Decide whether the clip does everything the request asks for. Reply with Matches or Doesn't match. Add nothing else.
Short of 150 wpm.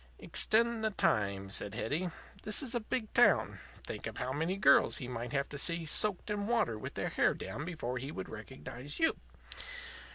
Doesn't match